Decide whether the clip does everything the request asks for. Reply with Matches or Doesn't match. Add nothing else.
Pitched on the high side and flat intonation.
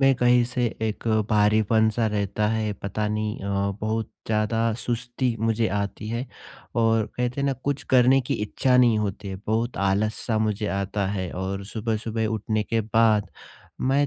Doesn't match